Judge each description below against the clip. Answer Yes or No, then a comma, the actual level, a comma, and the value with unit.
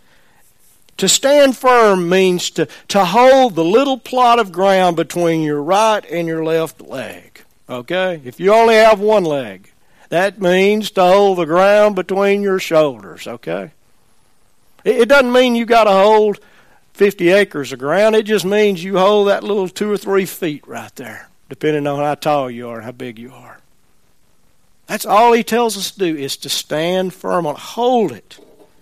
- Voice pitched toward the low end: No, high, 190 Hz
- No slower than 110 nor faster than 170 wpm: No, average, 180 wpm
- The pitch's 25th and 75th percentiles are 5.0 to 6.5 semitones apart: Yes, wide, 5.6 semitones